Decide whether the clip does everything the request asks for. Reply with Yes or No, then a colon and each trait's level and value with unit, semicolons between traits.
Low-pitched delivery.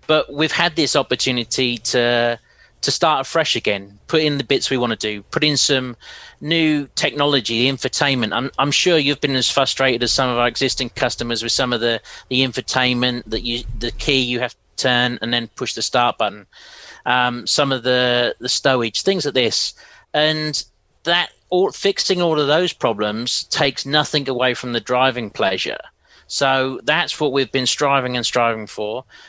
Yes: low, 130 Hz